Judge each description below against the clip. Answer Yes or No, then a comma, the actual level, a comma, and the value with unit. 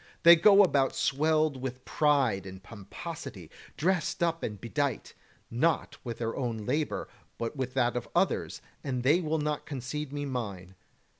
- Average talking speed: Yes, average, 155 wpm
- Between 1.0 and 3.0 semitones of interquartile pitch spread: No, average, 4.7 semitones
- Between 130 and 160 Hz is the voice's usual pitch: Yes, low, 135 Hz